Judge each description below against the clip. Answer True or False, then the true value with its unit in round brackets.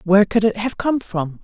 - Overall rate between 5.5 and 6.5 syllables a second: False (5.3 syllables/s)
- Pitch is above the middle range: True (205 Hz)